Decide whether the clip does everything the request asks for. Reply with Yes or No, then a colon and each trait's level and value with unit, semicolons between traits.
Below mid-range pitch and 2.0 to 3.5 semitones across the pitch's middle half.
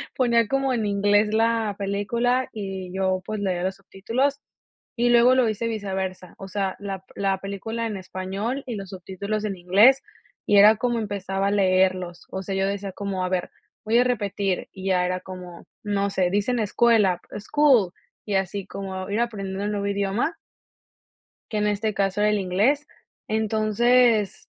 No: high, 200 Hz; average, 2.8 semitones